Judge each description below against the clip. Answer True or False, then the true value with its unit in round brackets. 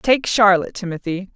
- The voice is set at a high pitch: True (195 Hz)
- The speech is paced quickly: False (135 wpm)